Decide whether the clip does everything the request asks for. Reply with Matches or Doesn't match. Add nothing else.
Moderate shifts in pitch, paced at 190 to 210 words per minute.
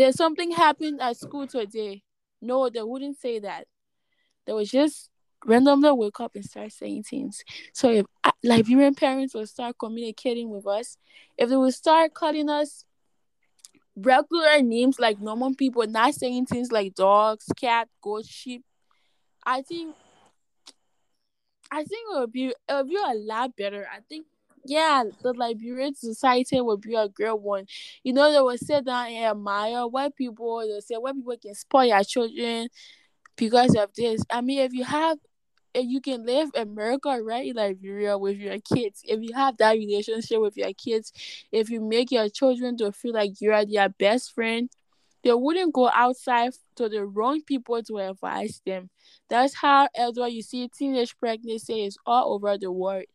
Doesn't match